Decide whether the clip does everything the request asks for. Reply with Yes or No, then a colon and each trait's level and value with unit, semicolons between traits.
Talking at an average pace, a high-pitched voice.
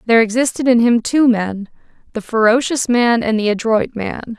Yes: average, 180 wpm; high, 230 Hz